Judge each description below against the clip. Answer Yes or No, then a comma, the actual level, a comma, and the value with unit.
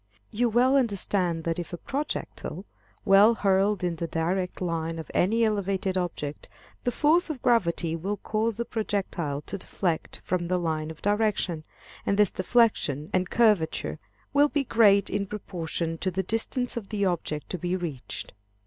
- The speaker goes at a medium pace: Yes, average, 165 wpm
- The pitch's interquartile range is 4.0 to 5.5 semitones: Yes, average, 4.5 semitones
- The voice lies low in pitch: No, high, 190 Hz